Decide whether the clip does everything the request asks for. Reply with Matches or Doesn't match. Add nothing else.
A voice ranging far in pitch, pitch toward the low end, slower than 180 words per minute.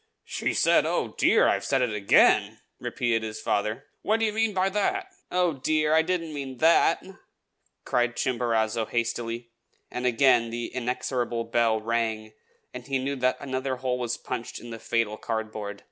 Doesn't match